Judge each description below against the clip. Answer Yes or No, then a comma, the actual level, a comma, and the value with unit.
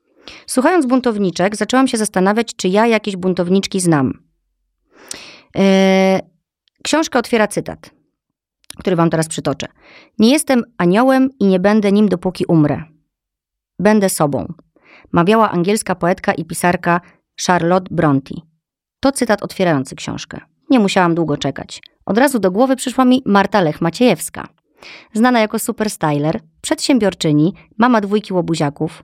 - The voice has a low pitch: No, high, 190 Hz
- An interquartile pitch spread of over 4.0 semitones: Yes, average, 5.1 semitones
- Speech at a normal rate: Yes, average, 125 wpm